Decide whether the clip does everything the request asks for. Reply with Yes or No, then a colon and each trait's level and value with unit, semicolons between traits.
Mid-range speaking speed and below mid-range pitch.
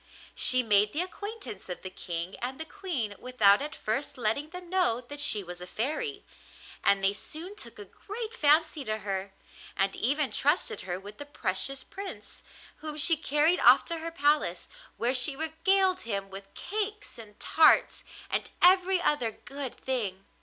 No: average, 170 wpm; very high, 285 Hz